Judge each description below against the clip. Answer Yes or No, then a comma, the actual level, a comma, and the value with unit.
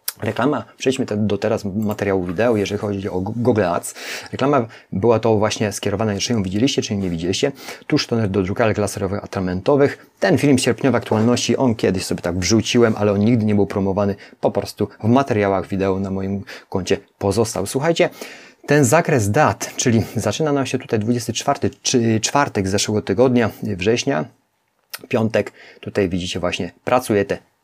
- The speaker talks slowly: No, fast, 160 wpm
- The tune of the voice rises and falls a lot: No, average, 3.6 semitones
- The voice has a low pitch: Yes, low, 105 Hz